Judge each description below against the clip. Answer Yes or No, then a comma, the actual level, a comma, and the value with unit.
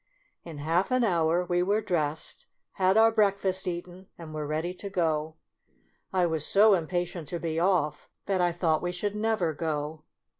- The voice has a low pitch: No, medium, 175 Hz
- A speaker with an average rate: No, fast, 210 wpm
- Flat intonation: No, average, 3.2 semitones